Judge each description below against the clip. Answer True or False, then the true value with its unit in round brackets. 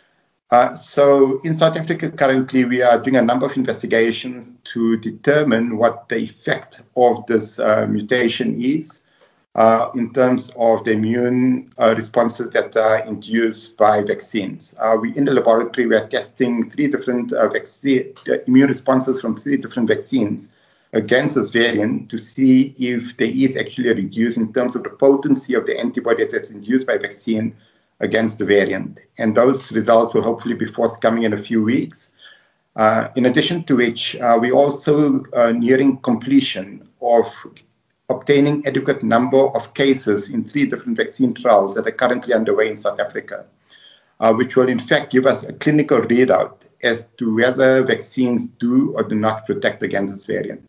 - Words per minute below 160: False (170 wpm)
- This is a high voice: False (125 Hz)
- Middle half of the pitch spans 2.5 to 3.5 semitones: True (3.1 semitones)